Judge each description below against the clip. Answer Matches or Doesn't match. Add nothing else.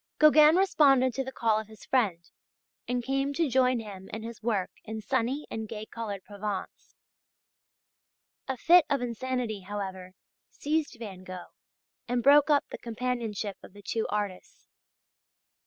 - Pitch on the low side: Doesn't match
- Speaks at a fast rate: Doesn't match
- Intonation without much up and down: Doesn't match